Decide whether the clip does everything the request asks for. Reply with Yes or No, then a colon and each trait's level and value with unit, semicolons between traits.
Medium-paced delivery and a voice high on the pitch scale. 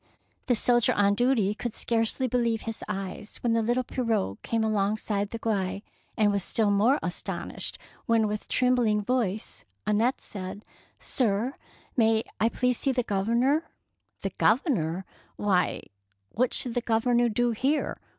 Yes: average, 155 wpm; high, 225 Hz